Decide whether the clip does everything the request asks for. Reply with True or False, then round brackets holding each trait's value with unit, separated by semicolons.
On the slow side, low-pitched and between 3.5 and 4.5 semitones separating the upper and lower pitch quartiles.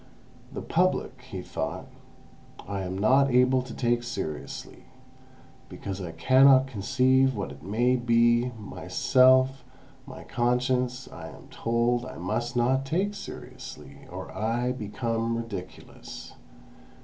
False (120 wpm; 120 Hz; 3.0 semitones)